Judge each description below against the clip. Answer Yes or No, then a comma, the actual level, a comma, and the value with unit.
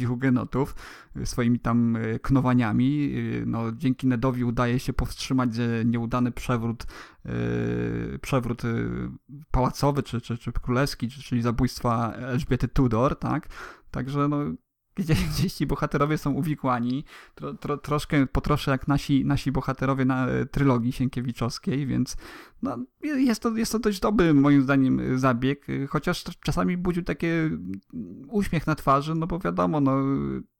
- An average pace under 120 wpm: No, average, 125 wpm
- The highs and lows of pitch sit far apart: No, average, 3.3 semitones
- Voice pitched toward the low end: Yes, low, 130 Hz